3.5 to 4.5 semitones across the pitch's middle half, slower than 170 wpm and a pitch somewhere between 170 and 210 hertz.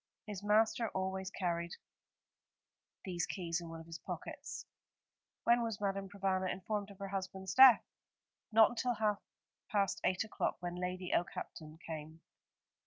No: average, 2.9 semitones; average, 140 wpm; high, 190 Hz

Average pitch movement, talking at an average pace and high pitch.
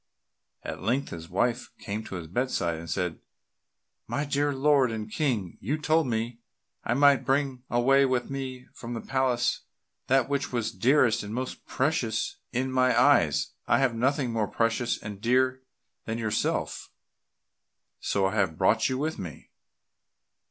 No: average, 3.6 semitones; average, 155 wpm; low, 125 Hz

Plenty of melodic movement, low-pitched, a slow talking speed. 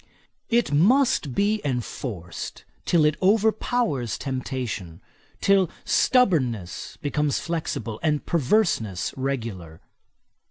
No: wide, 9.0 semitones; medium, 145 Hz; slow, 85 wpm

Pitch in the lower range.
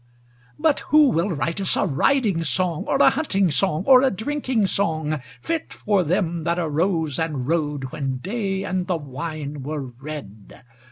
No: medium, 170 Hz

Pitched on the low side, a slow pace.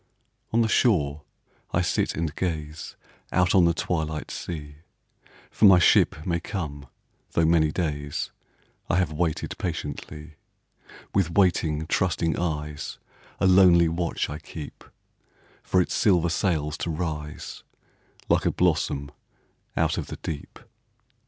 Yes: very low, 80 Hz; slow, 130 wpm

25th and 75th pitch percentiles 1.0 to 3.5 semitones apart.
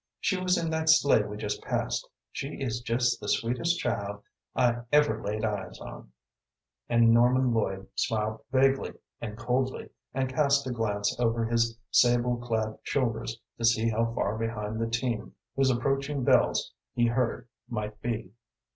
Yes: average, 2.9 semitones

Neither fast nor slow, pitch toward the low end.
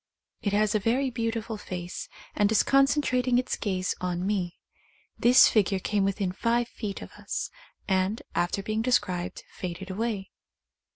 No: average, 150 wpm; high, 210 Hz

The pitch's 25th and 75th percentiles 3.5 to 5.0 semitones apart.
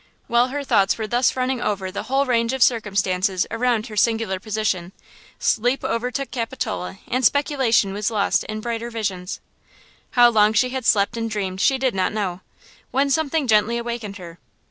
Yes: average, 3.8 semitones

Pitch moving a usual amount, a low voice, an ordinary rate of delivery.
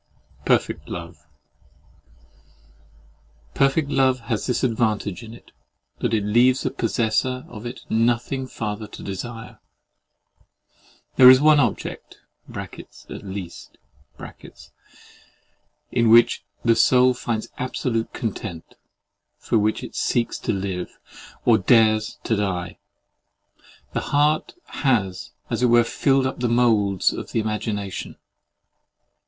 No: average, 3.4 semitones; low, 115 Hz; slow, 115 wpm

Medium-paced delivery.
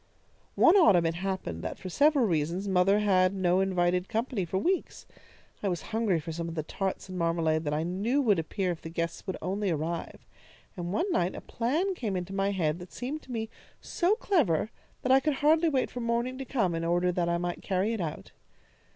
No: fast, 220 wpm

